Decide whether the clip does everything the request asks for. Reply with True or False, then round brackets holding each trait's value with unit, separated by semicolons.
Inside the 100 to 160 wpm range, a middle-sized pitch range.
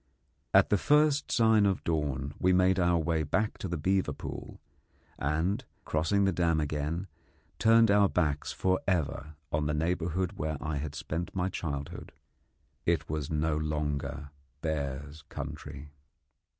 True (145 wpm; 3.9 semitones)